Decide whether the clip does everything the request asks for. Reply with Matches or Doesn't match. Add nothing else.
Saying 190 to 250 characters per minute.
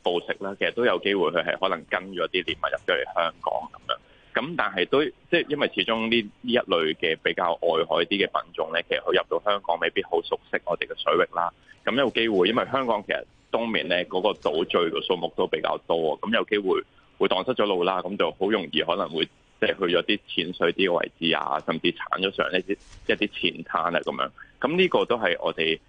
Doesn't match